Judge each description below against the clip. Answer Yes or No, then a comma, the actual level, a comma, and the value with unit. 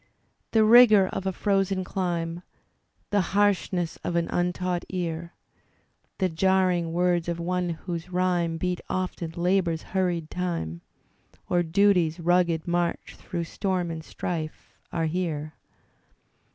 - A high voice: No, medium, 175 Hz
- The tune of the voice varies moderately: No, narrow, 1.8 semitones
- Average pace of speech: No, slow, 125 wpm